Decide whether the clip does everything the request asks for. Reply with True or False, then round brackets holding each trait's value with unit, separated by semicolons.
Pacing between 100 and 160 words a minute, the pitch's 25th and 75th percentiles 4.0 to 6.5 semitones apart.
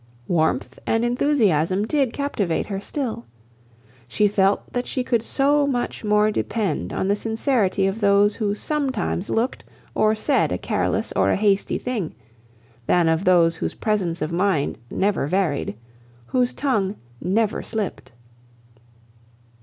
True (140 wpm; 4.7 semitones)